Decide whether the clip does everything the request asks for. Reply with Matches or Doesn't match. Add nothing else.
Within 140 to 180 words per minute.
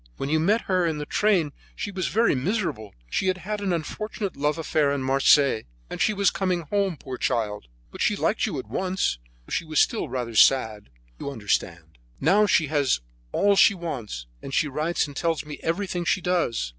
Doesn't match